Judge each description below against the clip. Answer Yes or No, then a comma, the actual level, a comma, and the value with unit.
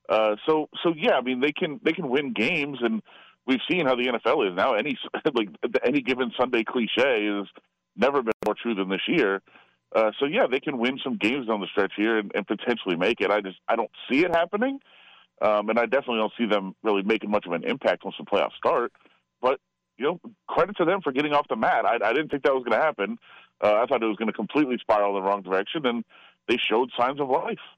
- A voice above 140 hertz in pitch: No, low, 115 Hz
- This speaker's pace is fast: Yes, fast, 245 wpm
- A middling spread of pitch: No, wide, 5.8 semitones